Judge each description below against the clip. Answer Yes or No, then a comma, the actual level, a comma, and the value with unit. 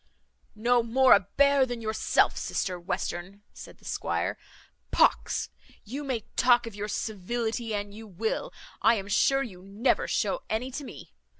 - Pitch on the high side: Yes, high, 225 Hz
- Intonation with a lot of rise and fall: No, average, 3.6 semitones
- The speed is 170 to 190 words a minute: No, average, 160 wpm